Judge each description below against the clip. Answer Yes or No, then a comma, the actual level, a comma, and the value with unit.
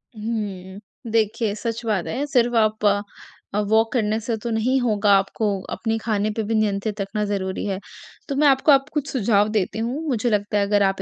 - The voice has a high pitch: Yes, high, 220 Hz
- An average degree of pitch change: No, narrow, 2.3 semitones